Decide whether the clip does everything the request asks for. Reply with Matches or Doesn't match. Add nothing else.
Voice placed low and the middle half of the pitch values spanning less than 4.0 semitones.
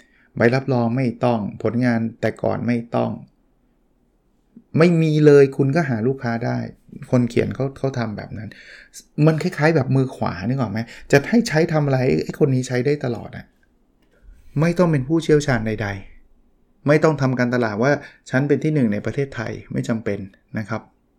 Doesn't match